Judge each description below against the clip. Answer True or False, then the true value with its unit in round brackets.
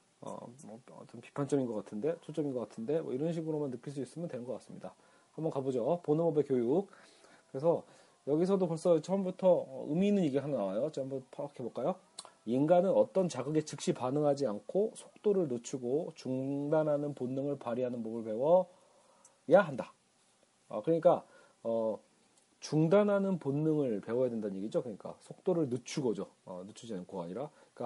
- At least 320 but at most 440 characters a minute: True (350 characters per minute)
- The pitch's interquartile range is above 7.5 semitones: False (5.2 semitones)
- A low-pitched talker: False (150 Hz)